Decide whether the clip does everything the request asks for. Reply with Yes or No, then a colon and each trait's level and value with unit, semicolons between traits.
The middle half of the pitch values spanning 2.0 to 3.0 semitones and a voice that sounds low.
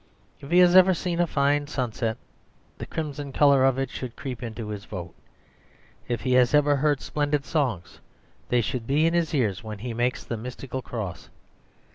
No: average, 4.0 semitones; low, 130 Hz